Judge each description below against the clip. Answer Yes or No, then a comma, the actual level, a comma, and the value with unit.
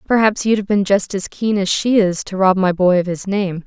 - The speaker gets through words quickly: Yes, fast, 280 wpm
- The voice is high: Yes, high, 195 Hz